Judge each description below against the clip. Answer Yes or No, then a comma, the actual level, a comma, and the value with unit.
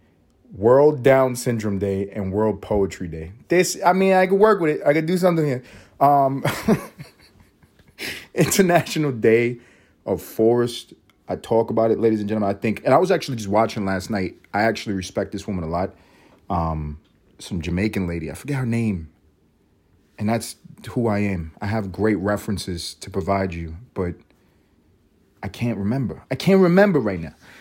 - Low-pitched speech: Yes, low, 105 Hz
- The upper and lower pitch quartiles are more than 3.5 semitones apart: Yes, average, 4.9 semitones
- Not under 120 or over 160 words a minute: No, average, 170 wpm